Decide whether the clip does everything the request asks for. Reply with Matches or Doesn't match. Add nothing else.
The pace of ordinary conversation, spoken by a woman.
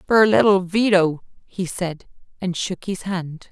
Matches